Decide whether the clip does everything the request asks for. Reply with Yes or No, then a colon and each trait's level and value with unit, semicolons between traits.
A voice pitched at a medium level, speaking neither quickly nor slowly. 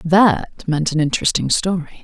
Yes: medium, 170 Hz; average, 145 wpm